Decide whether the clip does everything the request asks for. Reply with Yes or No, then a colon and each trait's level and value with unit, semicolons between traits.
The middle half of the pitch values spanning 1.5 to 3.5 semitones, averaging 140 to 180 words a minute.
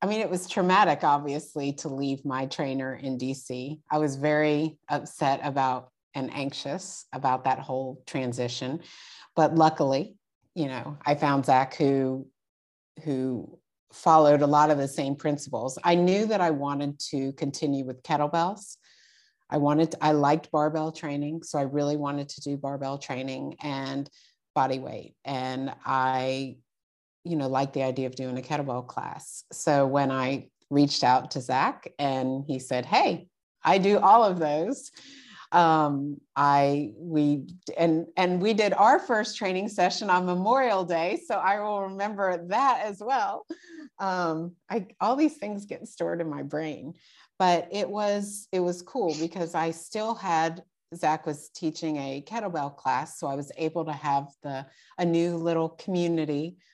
No: average, 4.1 semitones; average, 160 wpm